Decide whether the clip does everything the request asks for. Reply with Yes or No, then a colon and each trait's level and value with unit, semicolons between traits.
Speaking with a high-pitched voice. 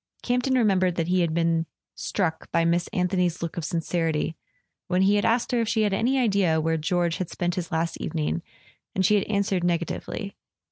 No: medium, 180 Hz